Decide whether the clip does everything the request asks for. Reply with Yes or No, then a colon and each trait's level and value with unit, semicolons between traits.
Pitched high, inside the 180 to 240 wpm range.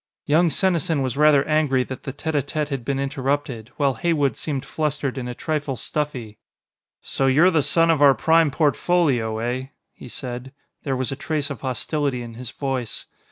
No: medium, 140 Hz; average, 185 wpm